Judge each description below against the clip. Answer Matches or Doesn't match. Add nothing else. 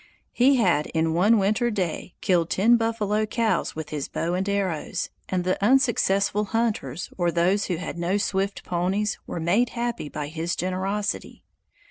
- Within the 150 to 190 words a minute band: Matches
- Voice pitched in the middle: Doesn't match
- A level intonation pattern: Doesn't match